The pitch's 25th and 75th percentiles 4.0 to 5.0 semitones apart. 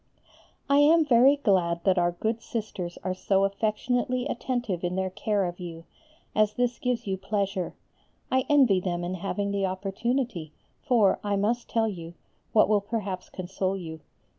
Yes: average, 4.4 semitones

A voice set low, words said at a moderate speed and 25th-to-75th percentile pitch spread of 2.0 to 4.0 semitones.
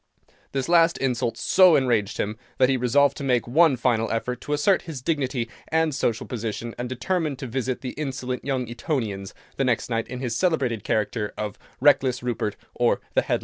Yes: low, 125 Hz; average, 190 wpm; average, 3.4 semitones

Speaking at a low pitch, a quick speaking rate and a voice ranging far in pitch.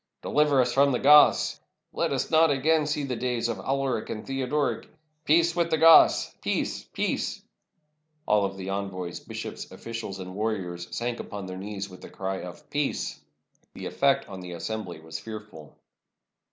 No: low, 110 Hz; average, 170 wpm; wide, 6.6 semitones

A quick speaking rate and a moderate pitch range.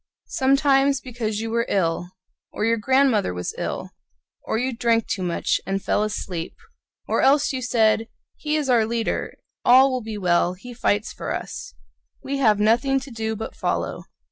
No: average, 175 wpm; average, 4.0 semitones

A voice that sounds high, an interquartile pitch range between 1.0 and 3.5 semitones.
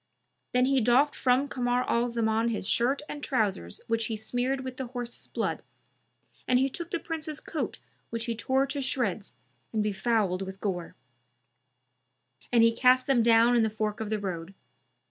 Yes: high, 235 Hz; average, 3.1 semitones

